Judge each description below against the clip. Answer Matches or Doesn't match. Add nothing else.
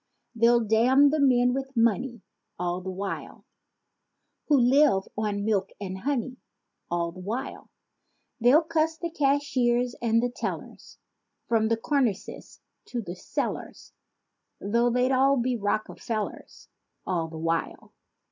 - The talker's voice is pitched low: Doesn't match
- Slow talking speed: Matches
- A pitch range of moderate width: Matches